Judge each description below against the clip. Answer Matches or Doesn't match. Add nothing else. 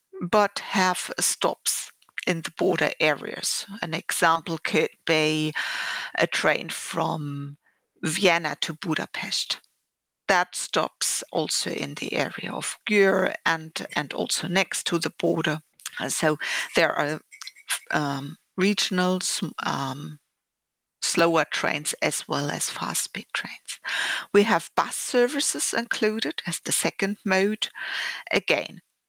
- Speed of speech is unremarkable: Doesn't match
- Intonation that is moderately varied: Matches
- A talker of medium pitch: Matches